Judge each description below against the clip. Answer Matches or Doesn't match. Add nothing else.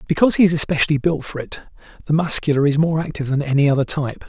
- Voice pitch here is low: Doesn't match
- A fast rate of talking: Matches